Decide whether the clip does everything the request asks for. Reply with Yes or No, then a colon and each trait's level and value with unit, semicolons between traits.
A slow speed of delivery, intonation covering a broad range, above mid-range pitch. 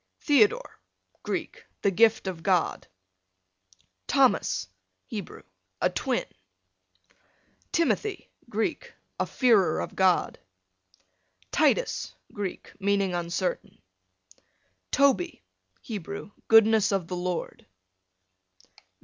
No: slow, 80 wpm; average, 3.9 semitones; high, 200 Hz